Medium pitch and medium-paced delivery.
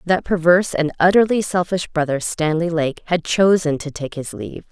Yes: medium, 165 Hz; average, 180 wpm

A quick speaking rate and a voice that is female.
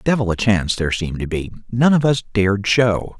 No: fast, 225 wpm; male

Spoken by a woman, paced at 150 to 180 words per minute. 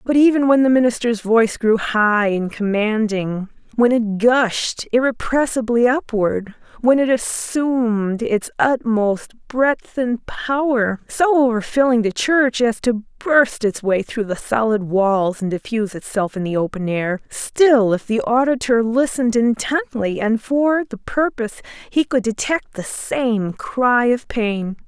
No: female; average, 140 wpm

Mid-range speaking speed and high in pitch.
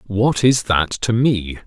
No: average, 180 wpm; low, 110 Hz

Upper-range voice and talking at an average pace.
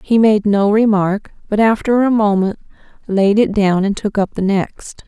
Yes: high, 205 Hz; average, 190 wpm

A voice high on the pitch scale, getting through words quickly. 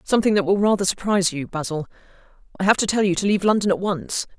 Yes: high, 195 Hz; fast, 235 wpm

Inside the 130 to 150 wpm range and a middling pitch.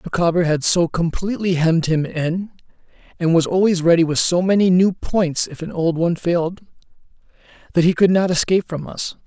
No: average, 180 wpm; medium, 175 Hz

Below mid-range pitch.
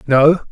No: medium, 150 Hz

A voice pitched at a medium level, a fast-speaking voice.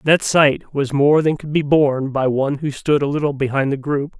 Yes: medium, 145 Hz; fast, 245 wpm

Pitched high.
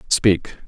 No: low, 100 Hz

